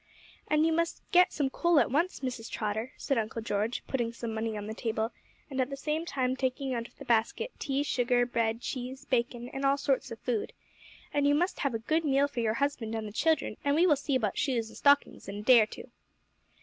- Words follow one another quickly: Yes, fast, 235 wpm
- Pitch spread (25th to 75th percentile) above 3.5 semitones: Yes, average, 4.0 semitones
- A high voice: Yes, very high, 255 Hz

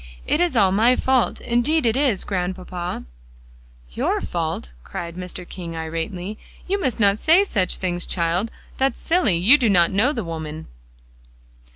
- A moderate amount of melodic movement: No, wide, 6.4 semitones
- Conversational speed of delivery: Yes, average, 150 wpm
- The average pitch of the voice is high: Yes, high, 195 Hz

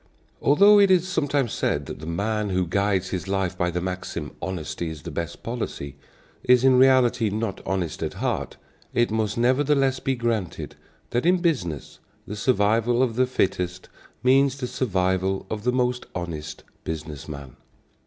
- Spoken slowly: No, average, 165 wpm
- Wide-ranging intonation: Yes, wide, 6.0 semitones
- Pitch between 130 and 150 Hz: No, low, 105 Hz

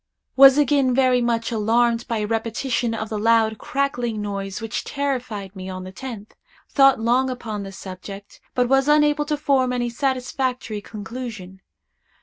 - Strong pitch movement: No, average, 3.8 semitones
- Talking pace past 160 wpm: No, average, 155 wpm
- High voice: Yes, high, 235 Hz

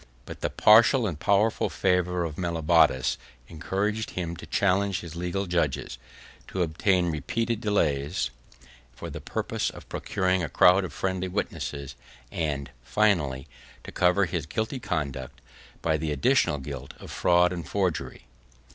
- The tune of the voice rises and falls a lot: No, average, 4.6 semitones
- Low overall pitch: Yes, very low, 90 Hz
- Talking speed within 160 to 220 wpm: No, average, 140 wpm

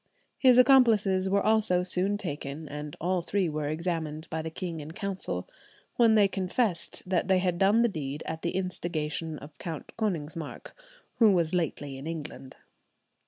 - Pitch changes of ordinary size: Yes, average, 4.1 semitones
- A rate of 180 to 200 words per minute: No, average, 165 wpm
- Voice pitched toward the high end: No, medium, 175 Hz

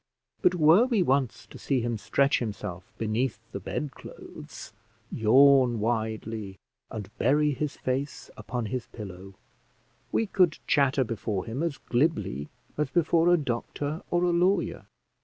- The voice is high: No, low, 130 Hz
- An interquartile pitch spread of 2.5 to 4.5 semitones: No, wide, 5.6 semitones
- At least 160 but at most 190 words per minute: No, average, 140 wpm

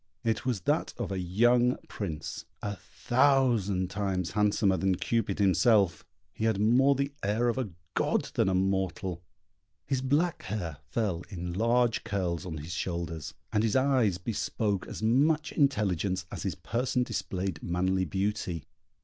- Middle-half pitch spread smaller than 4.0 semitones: No, average, 4.7 semitones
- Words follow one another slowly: No, average, 150 wpm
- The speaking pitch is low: Yes, low, 100 Hz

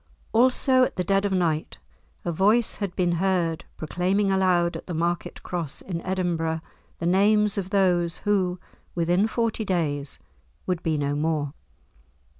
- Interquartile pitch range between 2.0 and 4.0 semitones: Yes, average, 2.9 semitones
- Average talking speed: Yes, average, 150 wpm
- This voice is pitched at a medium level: Yes, medium, 180 Hz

